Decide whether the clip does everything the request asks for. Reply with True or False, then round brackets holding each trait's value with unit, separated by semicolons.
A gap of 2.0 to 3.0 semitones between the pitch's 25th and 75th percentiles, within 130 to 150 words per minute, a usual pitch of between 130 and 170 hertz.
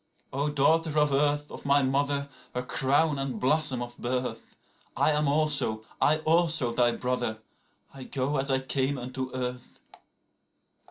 True (2.6 semitones; 145 wpm; 135 Hz)